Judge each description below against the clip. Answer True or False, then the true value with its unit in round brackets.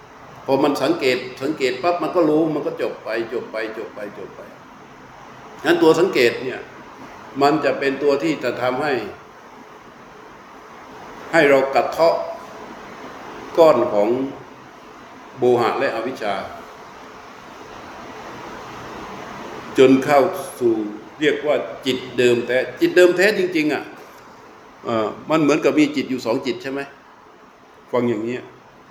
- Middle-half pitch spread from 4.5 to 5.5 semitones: True (5.1 semitones)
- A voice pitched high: False (135 Hz)